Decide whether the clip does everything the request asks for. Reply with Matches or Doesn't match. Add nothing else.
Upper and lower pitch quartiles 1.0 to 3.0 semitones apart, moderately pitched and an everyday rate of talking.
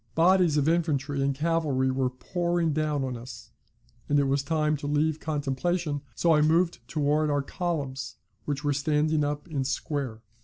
Matches